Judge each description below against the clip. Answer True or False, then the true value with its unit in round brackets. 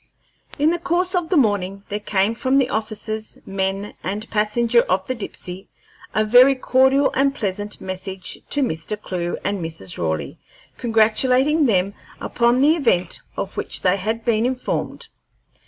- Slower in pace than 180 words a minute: True (155 wpm)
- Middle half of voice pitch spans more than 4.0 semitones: True (5.1 semitones)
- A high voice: True (215 Hz)